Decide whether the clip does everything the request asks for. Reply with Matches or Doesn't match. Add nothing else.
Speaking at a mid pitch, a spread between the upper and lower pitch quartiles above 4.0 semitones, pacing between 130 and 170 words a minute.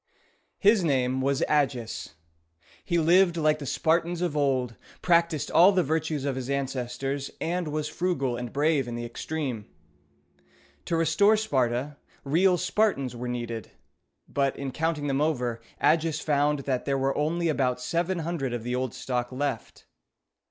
Matches